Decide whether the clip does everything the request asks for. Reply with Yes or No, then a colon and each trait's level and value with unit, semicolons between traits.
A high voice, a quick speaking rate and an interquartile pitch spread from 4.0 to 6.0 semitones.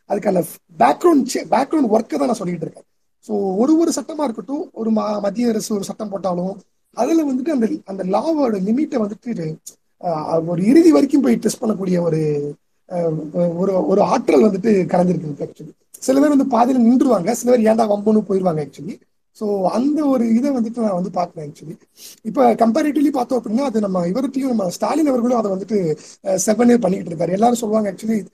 Yes: high, 220 Hz; fast, 155 wpm; average, 5.1 semitones